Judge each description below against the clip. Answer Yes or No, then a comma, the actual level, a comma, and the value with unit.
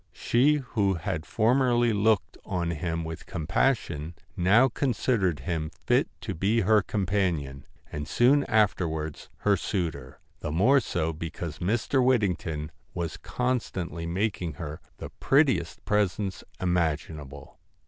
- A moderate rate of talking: No, slow, 130 wpm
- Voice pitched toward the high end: No, very low, 90 Hz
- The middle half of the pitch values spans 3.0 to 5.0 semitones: No, wide, 5.5 semitones